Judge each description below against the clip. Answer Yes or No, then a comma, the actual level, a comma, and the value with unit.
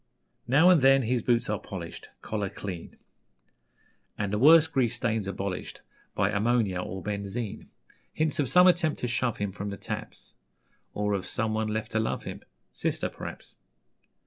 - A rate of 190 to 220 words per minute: No, average, 160 wpm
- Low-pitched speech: Yes, low, 110 Hz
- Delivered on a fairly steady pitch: No, average, 4.1 semitones